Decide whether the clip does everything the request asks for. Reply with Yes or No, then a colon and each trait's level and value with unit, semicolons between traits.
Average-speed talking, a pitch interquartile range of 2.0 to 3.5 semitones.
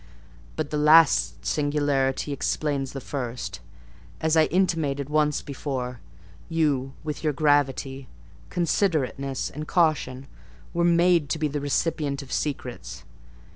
No: slow, 120 wpm; narrow, 2.5 semitones